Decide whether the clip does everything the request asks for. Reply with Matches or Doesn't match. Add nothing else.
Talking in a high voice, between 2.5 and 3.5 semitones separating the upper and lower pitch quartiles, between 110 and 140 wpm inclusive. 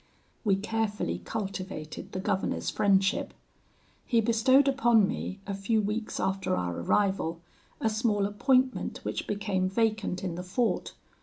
Matches